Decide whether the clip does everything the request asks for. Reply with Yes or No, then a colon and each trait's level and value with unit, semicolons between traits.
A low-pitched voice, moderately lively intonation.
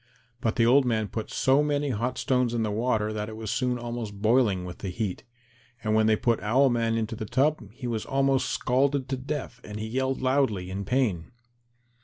Yes: low, 120 Hz; average, 3.5 semitones